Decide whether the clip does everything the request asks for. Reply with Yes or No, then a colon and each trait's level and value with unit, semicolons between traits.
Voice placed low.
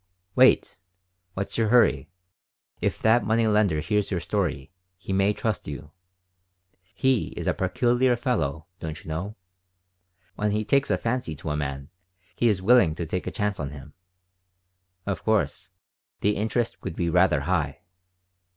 Yes: low, 100 Hz